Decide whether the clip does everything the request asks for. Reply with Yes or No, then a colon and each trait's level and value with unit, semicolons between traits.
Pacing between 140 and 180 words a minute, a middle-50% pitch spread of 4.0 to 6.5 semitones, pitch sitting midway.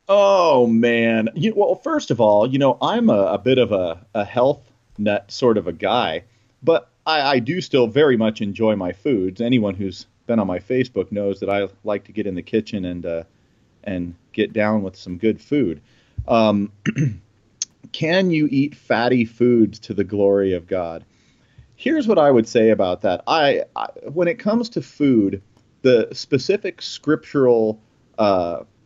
No: average, 175 wpm; average, 4.3 semitones; low, 110 Hz